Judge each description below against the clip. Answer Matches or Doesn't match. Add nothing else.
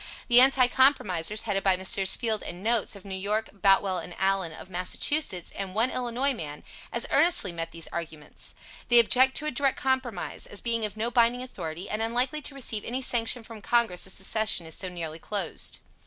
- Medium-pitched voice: Doesn't match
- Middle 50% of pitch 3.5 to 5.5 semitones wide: Matches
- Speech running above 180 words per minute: Matches